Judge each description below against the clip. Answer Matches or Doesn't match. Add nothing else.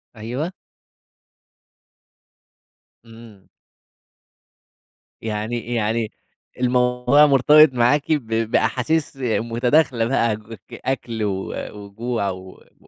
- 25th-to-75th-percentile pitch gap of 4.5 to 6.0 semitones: Doesn't match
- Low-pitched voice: Matches